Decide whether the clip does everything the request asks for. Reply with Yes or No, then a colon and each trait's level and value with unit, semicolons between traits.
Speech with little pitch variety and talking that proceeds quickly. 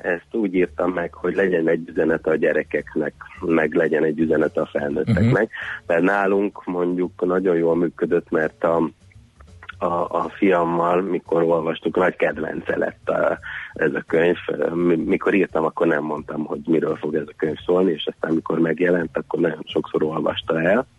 Yes: narrow, 1.7 semitones; fast, 165 wpm